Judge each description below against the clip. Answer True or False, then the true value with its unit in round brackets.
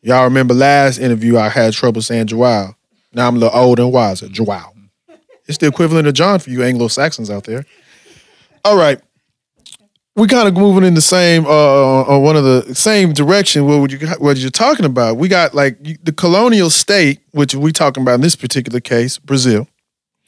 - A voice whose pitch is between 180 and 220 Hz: False (140 Hz)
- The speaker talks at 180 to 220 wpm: True (190 wpm)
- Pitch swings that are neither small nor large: True (4.7 semitones)